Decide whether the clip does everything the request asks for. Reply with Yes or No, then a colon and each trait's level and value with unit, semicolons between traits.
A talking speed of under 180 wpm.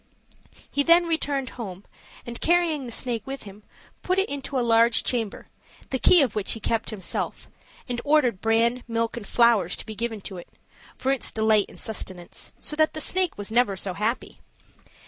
No: average, 185 wpm